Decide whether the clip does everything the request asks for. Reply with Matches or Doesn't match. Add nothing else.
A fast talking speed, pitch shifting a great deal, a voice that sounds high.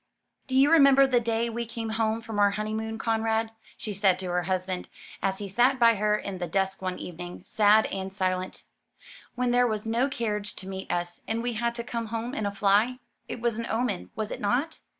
Doesn't match